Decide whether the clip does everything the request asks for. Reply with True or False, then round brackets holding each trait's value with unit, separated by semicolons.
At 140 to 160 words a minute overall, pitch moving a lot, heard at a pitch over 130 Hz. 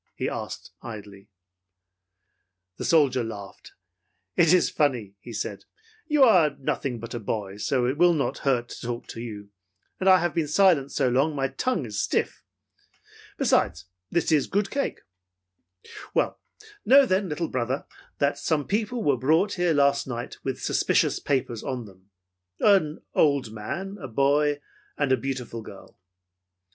True (155 wpm; 6.1 semitones; 140 Hz)